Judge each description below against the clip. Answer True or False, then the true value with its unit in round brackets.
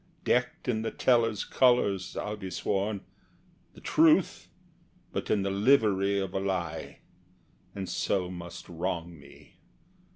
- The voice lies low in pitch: True (100 Hz)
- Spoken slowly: True (130 wpm)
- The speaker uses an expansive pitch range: False (3.5 semitones)